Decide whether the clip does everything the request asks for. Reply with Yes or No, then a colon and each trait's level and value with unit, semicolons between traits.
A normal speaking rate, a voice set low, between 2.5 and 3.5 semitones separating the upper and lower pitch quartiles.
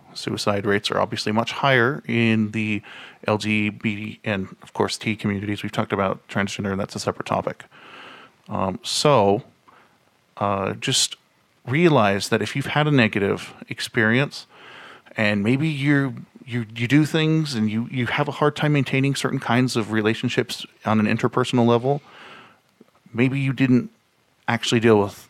No: average, 150 wpm; low, 115 Hz; average, 4.1 semitones